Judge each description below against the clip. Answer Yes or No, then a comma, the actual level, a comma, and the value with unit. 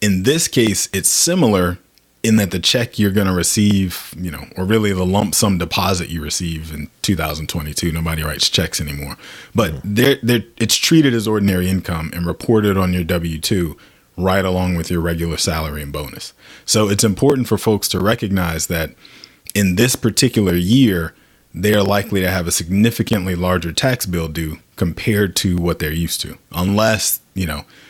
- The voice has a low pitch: Yes, very low, 95 Hz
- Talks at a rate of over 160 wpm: Yes, average, 175 wpm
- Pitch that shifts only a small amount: No, average, 4.1 semitones